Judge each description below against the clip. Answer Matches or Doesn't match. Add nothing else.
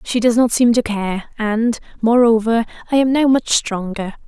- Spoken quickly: Doesn't match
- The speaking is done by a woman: Matches